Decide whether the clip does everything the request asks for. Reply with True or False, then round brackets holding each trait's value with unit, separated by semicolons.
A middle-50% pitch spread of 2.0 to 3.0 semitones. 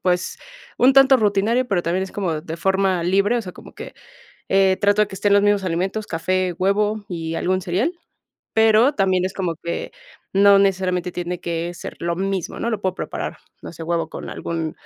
True (2.6 semitones)